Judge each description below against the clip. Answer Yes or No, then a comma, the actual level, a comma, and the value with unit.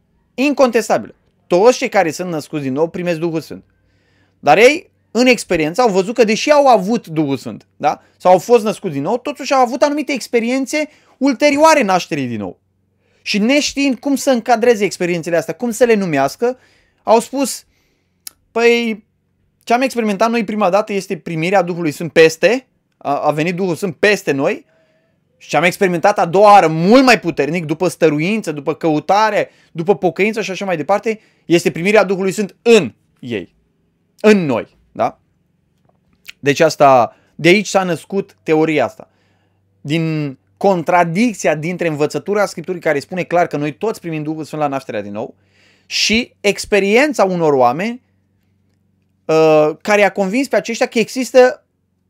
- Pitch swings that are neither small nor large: No, wide, 6.6 semitones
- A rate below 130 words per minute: No, average, 155 wpm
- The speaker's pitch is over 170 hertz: Yes, medium, 185 Hz